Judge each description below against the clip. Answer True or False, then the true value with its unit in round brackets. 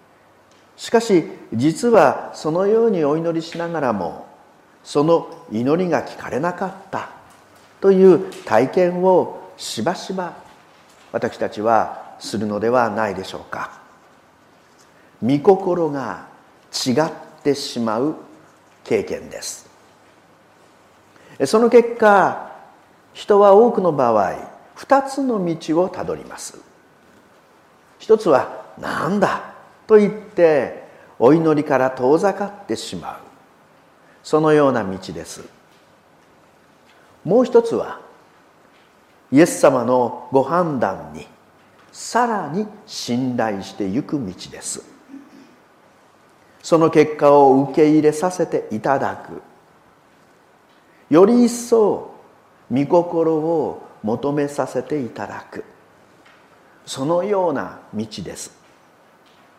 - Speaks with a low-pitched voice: False (165 Hz)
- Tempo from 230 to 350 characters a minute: False (185 characters per minute)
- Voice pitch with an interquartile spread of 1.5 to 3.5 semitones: False (7.2 semitones)